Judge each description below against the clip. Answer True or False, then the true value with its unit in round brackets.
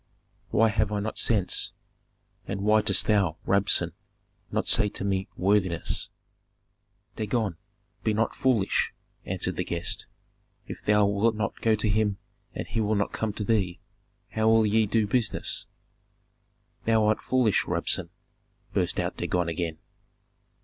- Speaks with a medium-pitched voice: False (105 Hz)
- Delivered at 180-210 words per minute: False (140 wpm)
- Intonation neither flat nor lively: False (1.9 semitones)